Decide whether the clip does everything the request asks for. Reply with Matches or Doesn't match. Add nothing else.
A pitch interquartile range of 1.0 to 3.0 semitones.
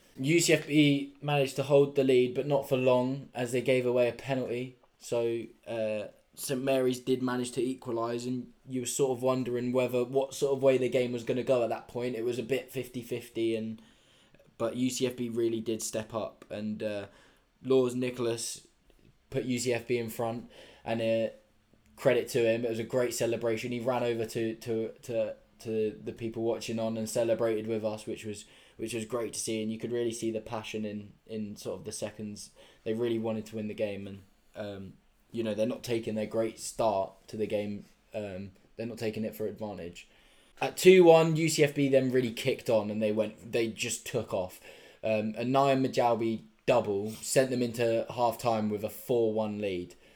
Matches